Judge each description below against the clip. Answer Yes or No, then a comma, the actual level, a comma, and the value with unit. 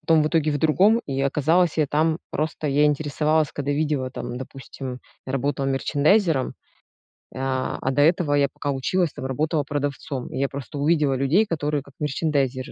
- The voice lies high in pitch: No, medium, 145 Hz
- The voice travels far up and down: No, narrow, 2.6 semitones